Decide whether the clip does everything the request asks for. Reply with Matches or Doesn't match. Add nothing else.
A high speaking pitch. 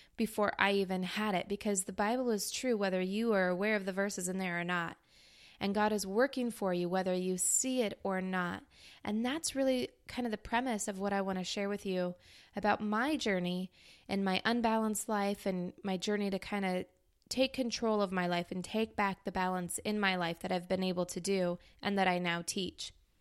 Matches